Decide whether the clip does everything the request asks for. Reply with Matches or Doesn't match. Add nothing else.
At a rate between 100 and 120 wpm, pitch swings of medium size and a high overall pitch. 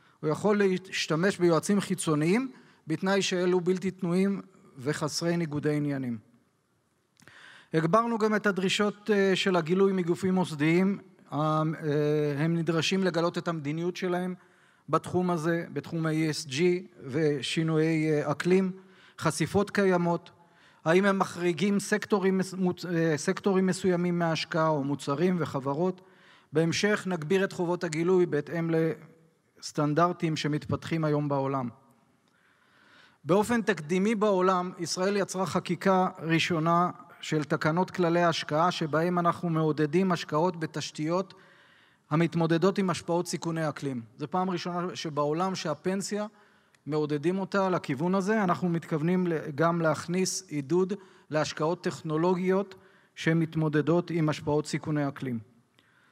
Doesn't match